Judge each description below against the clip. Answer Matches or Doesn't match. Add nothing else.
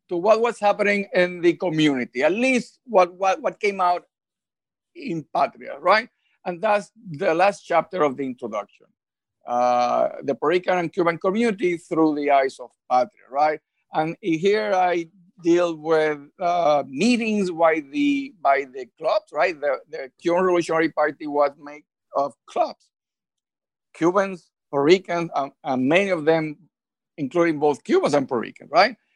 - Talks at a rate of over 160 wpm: Doesn't match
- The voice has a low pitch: Doesn't match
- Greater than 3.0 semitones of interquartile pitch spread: Matches